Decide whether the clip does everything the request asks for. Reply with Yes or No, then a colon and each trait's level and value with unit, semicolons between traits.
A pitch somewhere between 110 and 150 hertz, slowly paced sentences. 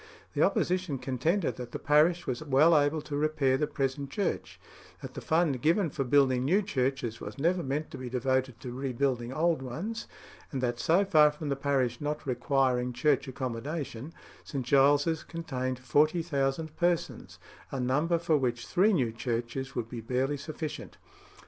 No: medium, 140 Hz; average, 165 wpm